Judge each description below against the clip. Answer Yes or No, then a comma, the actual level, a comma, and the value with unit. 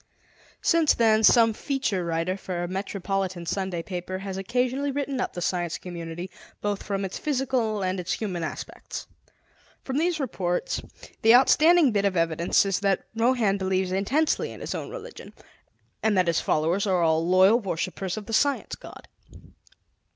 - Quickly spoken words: No, average, 160 wpm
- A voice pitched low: No, high, 195 Hz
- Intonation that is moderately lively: Yes, average, 5.0 semitones